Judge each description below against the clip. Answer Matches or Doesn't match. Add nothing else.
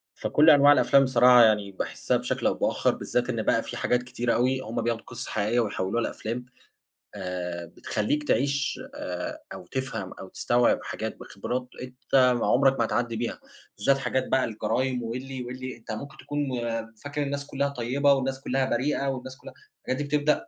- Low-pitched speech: Matches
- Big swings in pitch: Doesn't match